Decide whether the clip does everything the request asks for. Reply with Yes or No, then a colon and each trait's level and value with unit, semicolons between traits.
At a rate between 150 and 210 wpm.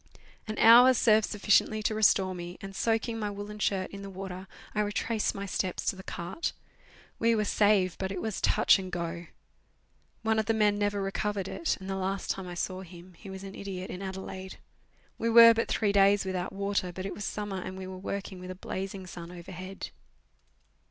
Yes: fast, 205 wpm